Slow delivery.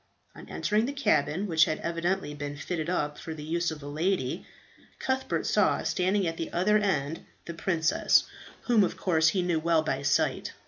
No: average, 185 wpm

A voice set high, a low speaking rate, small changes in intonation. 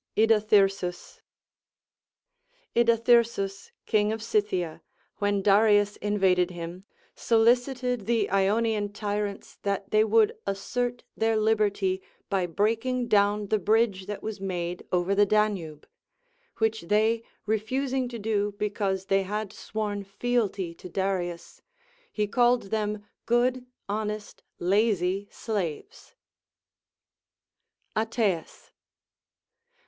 Yes: high, 210 Hz; slow, 100 wpm; narrow, 2.3 semitones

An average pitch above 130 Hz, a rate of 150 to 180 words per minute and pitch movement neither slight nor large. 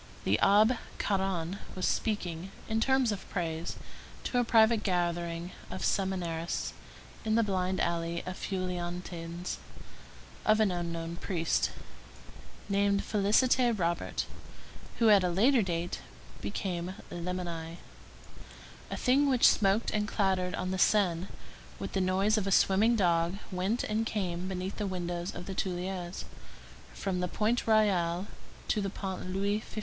No: high, 190 Hz; average, 140 wpm; average, 3.2 semitones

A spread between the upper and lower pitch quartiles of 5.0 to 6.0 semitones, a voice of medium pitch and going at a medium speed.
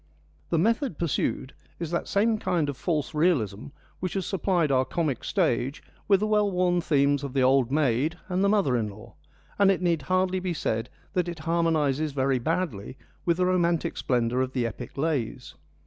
Yes: wide, 5.5 semitones; medium, 160 Hz; average, 185 wpm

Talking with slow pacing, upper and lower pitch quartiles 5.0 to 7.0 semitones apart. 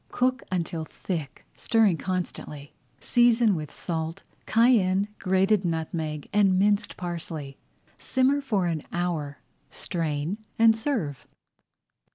Yes: slow, 105 wpm; average, 5.3 semitones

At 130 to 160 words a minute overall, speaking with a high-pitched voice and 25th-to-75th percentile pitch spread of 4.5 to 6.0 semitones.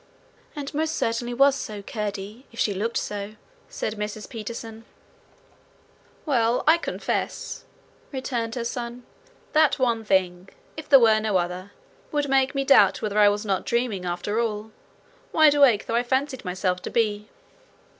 No: average, 155 wpm; high, 230 Hz; average, 4.1 semitones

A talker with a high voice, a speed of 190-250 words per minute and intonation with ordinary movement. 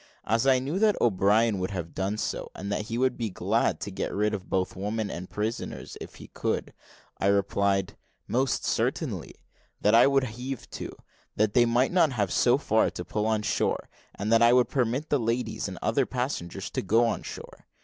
No: low, 110 Hz; average, 200 wpm; average, 3.8 semitones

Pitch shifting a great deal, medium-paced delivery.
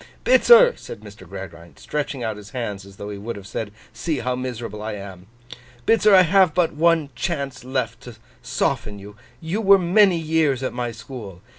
Yes: wide, 7.9 semitones; average, 185 wpm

